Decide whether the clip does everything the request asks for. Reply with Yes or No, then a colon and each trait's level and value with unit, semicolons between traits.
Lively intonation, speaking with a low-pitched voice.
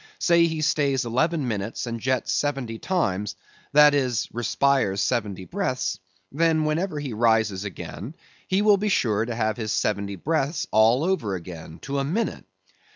Yes: wide, 6.4 semitones; low, 125 Hz